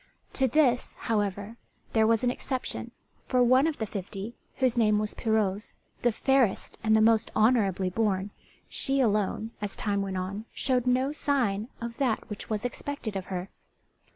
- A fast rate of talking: No, average, 165 wpm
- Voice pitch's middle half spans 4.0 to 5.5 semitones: No, average, 3.6 semitones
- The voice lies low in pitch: No, high, 220 Hz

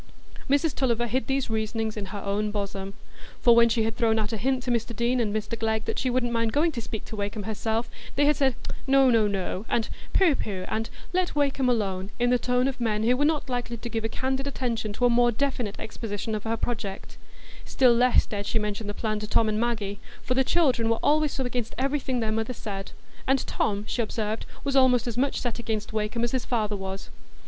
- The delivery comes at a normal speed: No, fast, 230 wpm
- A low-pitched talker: No, high, 230 Hz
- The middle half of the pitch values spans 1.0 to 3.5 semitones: Yes, average, 3.0 semitones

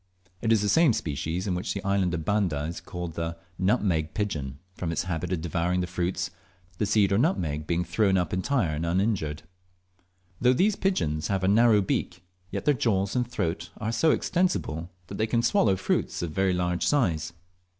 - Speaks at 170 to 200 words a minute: Yes, average, 190 wpm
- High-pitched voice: No, very low, 90 Hz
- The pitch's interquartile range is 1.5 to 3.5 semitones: No, average, 4.3 semitones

